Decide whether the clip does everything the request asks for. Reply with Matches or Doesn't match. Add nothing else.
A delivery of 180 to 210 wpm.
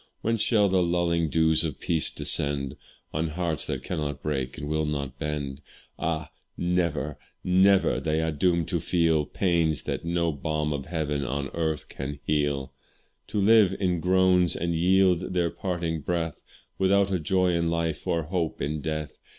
Doesn't match